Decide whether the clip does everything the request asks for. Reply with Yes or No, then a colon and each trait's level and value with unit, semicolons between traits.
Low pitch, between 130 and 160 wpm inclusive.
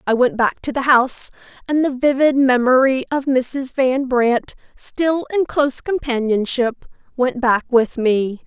No: very high, 260 Hz; average, 155 wpm